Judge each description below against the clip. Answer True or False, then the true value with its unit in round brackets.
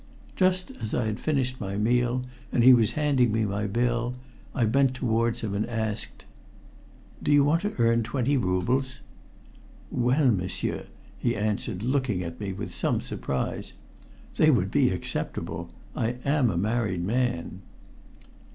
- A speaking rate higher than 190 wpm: False (150 wpm)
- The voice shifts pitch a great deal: False (3.7 semitones)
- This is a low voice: True (120 Hz)